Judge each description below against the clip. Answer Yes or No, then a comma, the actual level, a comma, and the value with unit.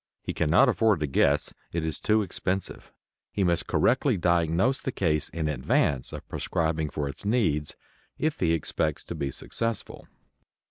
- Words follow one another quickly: No, average, 155 wpm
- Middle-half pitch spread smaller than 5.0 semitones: No, average, 5.3 semitones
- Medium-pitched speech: No, very low, 85 Hz